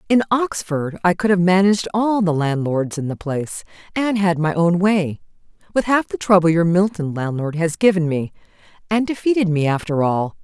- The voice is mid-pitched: Yes, medium, 180 Hz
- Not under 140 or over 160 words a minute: No, average, 185 wpm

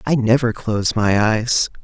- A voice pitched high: No, low, 115 Hz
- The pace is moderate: Yes, average, 165 wpm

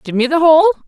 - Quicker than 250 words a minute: Yes, fast, 275 wpm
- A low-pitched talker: No, very high, 305 Hz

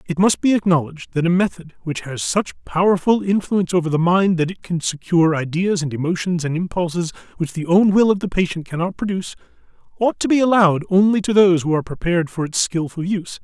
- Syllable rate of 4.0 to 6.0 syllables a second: No, 6.3 syllables/s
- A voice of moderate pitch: Yes, medium, 175 Hz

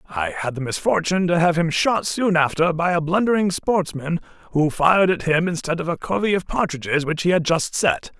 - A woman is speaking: No, male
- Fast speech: Yes, fast, 210 wpm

